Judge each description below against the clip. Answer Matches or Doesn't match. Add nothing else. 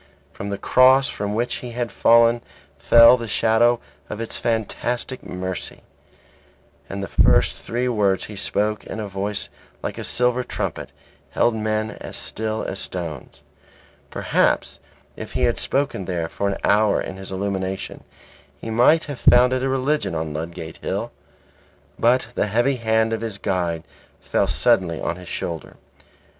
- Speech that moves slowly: Doesn't match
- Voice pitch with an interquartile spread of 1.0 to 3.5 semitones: Doesn't match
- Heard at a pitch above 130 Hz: Doesn't match